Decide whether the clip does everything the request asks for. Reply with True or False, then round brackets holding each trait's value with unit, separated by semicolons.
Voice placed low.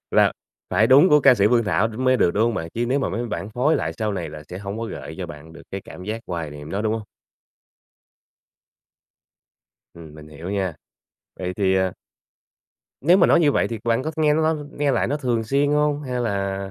True (110 Hz)